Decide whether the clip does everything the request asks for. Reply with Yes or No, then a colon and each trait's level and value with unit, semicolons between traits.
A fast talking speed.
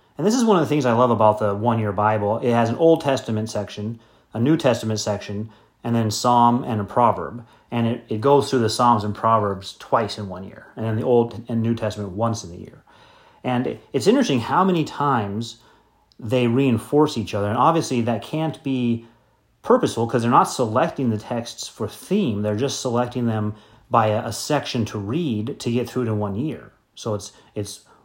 Yes: fast, 210 wpm